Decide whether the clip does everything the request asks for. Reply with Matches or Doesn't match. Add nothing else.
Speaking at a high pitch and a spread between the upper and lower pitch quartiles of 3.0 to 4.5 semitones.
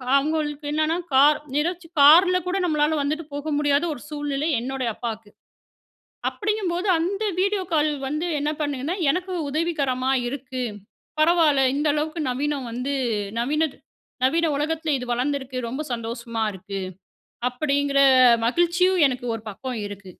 Matches